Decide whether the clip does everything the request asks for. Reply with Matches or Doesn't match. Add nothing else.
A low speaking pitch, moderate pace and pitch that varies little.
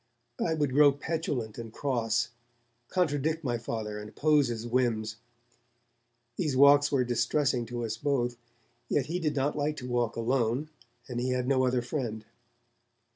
Doesn't match